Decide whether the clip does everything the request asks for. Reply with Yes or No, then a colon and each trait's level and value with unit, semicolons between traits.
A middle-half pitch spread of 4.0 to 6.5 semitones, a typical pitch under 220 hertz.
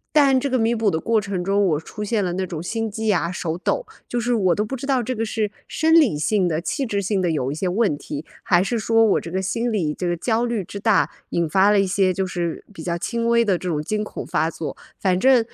Yes: average, 4.6 semitones; high, 200 Hz